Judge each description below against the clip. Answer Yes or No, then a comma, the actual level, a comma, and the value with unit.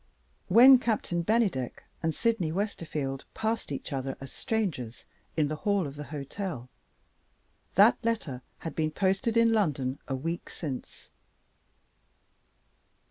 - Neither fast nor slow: No, slow, 125 wpm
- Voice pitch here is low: No, medium, 165 Hz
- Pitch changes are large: Yes, wide, 7.9 semitones